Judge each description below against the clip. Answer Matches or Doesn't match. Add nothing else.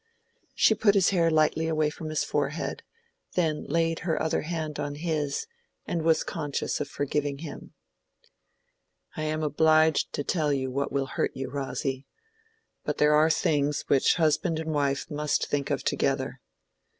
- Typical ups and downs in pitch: Doesn't match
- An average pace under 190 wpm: Matches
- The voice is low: Doesn't match